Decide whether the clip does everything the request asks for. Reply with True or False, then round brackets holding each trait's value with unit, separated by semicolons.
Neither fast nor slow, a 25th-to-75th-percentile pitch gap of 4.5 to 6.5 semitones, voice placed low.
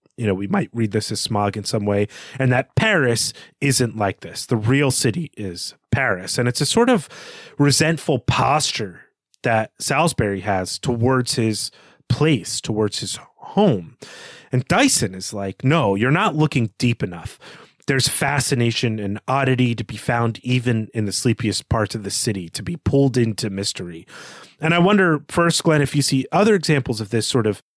True (175 wpm; 4.9 semitones; 125 Hz)